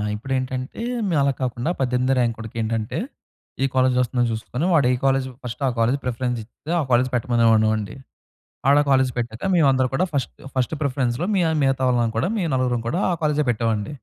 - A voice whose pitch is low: Yes, low, 125 Hz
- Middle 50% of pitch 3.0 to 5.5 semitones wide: No, narrow, 2.5 semitones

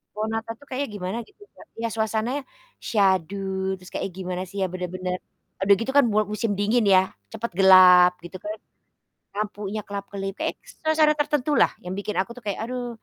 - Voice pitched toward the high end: Yes, high, 205 Hz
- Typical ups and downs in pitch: Yes, average, 3.6 semitones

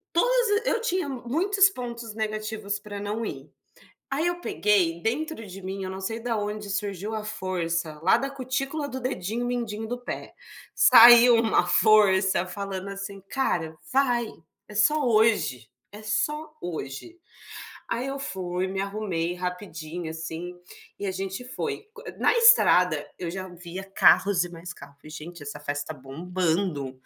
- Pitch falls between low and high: No, high, 205 Hz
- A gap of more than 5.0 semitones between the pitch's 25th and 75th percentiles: Yes, wide, 5.4 semitones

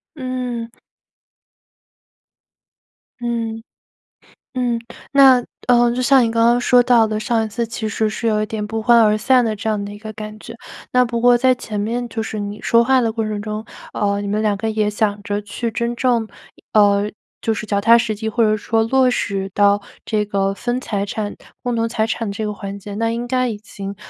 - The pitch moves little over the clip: Yes, narrow, 2.3 semitones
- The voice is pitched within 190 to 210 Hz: No, high, 220 Hz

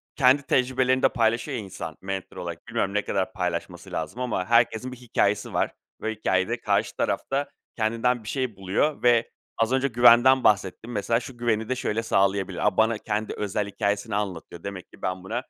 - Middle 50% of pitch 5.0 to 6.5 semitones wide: No, average, 3.9 semitones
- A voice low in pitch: Yes, low, 110 Hz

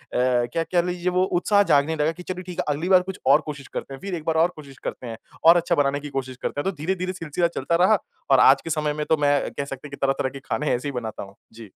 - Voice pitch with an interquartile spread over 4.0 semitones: Yes, average, 4.4 semitones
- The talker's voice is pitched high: No, medium, 150 Hz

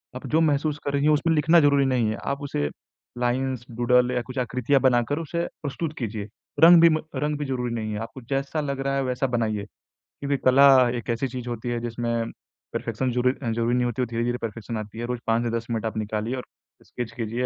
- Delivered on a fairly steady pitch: No, average, 3.1 semitones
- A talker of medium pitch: No, low, 125 Hz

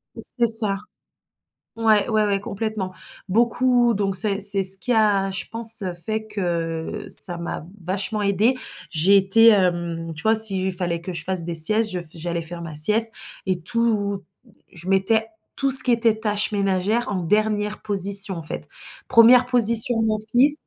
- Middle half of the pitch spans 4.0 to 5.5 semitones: No, average, 3.3 semitones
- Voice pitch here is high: Yes, high, 205 Hz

